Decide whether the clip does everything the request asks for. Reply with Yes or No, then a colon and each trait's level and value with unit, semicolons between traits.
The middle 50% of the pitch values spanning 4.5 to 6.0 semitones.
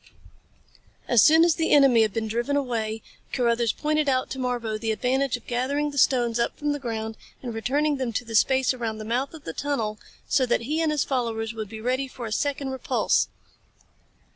No: average, 3.8 semitones